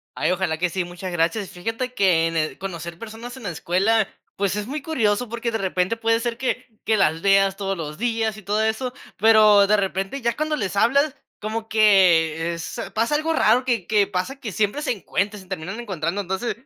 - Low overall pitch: No, high, 205 Hz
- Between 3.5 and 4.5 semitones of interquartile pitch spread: Yes, average, 3.8 semitones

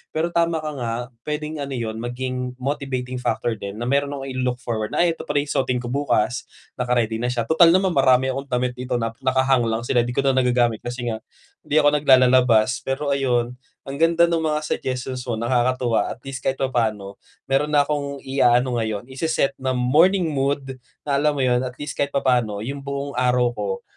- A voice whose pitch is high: No, low, 130 Hz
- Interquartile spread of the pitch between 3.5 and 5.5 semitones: No, narrow, 2.6 semitones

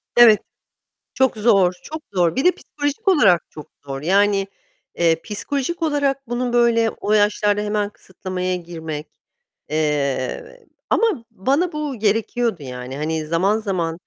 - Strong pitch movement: Yes, wide, 6.6 semitones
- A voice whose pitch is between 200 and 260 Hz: Yes, high, 205 Hz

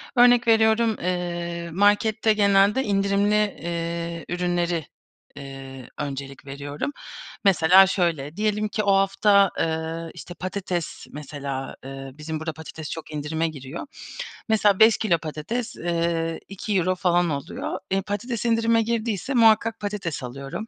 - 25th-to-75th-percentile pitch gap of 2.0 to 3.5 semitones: No, average, 4.8 semitones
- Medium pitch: Yes, medium, 175 Hz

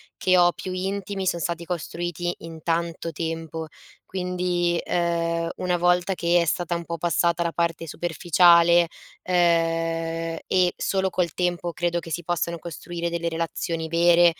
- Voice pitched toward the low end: No, medium, 170 Hz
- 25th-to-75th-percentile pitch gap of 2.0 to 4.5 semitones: No, narrow, 0.9 semitones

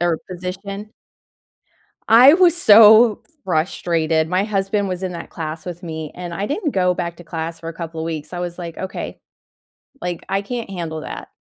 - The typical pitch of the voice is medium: Yes, medium, 180 Hz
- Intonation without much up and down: No, average, 3.3 semitones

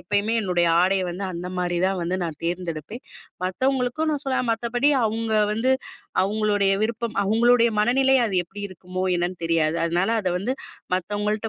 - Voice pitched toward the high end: Yes, high, 205 Hz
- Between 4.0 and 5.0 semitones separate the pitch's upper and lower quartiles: Yes, average, 4.4 semitones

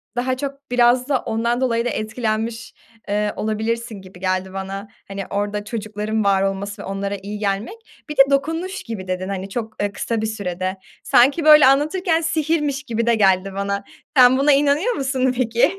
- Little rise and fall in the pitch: No, average, 5.2 semitones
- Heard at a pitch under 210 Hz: No, high, 225 Hz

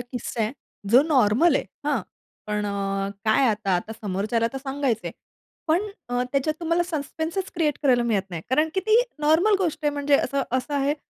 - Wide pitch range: Yes, wide, 6.2 semitones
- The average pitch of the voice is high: Yes, very high, 270 Hz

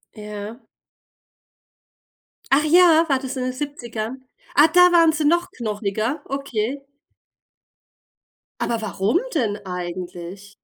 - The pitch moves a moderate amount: No, wide, 6.2 semitones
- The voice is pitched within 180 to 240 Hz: No, very high, 250 Hz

